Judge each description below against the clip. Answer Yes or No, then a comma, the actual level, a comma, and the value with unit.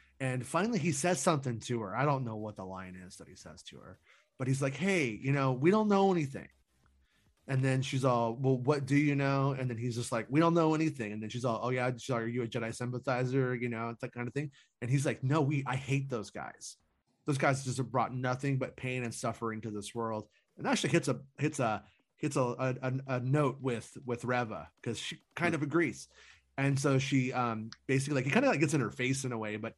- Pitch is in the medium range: No, low, 130 Hz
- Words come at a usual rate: No, fast, 250 wpm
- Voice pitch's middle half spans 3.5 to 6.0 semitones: No, average, 2.9 semitones